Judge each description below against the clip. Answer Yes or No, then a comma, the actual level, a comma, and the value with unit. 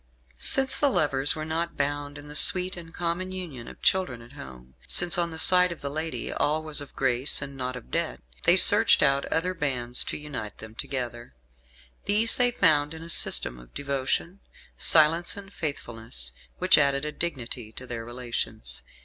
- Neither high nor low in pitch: Yes, medium, 145 Hz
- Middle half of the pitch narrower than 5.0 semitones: No, average, 5.3 semitones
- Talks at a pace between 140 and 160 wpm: No, average, 185 wpm